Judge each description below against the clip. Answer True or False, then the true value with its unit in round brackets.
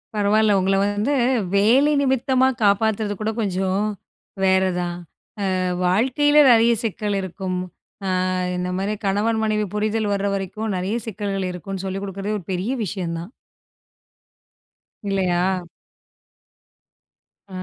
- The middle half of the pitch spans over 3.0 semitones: False (2.6 semitones)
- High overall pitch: True (200 Hz)